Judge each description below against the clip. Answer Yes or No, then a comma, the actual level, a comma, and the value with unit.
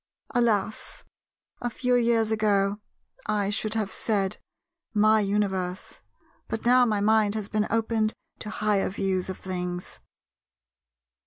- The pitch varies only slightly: Yes, narrow, 2.0 semitones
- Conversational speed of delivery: No, slow, 125 wpm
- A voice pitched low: No, high, 210 Hz